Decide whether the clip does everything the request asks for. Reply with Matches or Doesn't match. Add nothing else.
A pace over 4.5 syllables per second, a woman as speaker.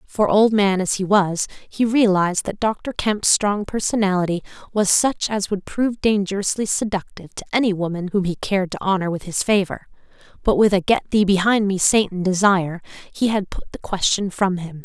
Matches